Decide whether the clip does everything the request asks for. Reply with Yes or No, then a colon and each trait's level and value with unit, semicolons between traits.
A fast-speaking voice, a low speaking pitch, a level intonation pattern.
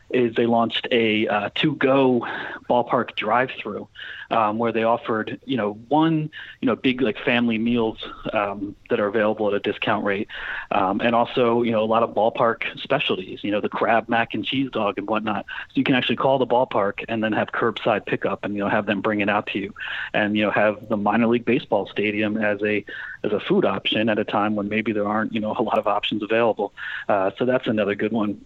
Yes: fast, 225 wpm; low, 115 Hz; narrow, 2.2 semitones